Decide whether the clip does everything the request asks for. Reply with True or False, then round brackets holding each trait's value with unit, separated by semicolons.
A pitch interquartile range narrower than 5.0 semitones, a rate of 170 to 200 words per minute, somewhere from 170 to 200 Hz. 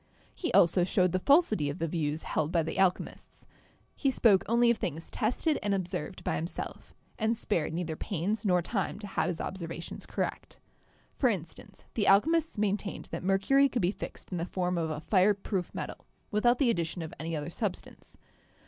True (4.5 semitones; 190 wpm; 190 Hz)